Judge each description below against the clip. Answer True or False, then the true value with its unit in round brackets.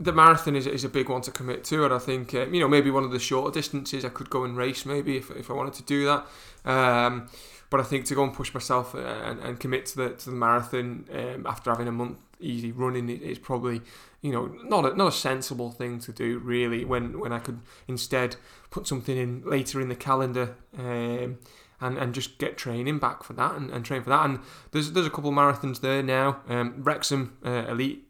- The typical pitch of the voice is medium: False (130 Hz)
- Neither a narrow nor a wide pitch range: False (2.0 semitones)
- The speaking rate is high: True (240 wpm)